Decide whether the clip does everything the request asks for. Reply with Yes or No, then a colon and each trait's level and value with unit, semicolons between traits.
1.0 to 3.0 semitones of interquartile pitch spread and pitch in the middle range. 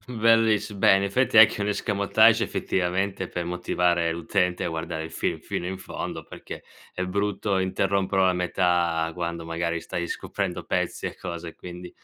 No: average, 2.7 semitones; very low, 90 Hz